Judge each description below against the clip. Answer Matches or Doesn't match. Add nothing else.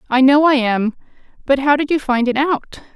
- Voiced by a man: Doesn't match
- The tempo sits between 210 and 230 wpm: Matches